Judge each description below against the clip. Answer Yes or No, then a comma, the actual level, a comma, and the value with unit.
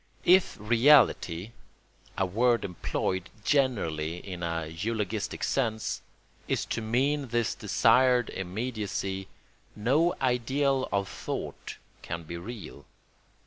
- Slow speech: Yes, slow, 100 wpm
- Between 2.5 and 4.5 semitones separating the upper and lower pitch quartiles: No, wide, 5.4 semitones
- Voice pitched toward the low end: Yes, low, 110 Hz